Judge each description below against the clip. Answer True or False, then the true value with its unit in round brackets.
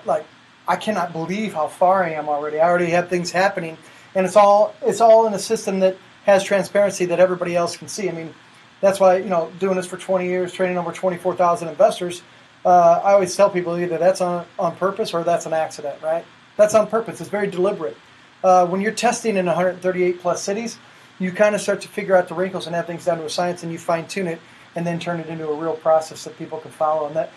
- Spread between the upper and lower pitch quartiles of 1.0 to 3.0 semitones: True (2.6 semitones)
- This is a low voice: False (180 Hz)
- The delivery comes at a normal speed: False (245 wpm)